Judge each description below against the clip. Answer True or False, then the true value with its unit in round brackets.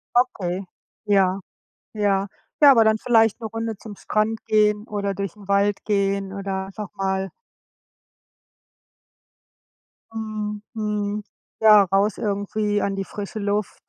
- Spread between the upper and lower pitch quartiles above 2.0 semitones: False (1.5 semitones)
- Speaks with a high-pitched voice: True (205 Hz)